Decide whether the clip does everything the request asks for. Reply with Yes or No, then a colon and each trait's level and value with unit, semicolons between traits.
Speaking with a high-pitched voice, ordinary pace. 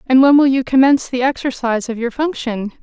No: very high, 255 Hz; fast, 210 wpm